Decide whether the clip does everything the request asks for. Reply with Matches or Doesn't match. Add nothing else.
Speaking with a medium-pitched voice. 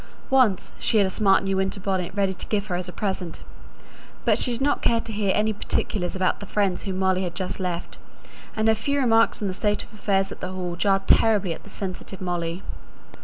Doesn't match